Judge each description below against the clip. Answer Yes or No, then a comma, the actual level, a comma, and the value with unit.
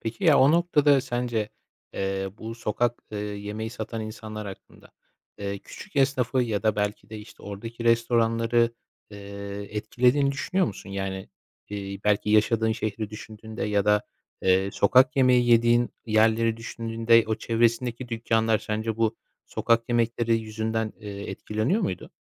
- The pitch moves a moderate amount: No, narrow, 2.1 semitones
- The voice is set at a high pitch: No, low, 110 Hz